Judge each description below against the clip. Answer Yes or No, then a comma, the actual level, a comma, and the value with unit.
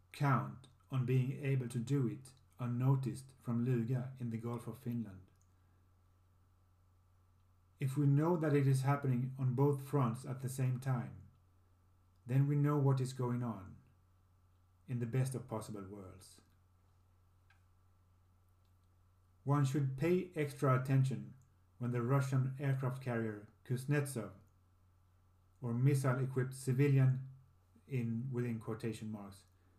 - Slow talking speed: Yes, slow, 125 wpm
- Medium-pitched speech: No, low, 120 Hz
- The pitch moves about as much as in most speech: No, wide, 6.5 semitones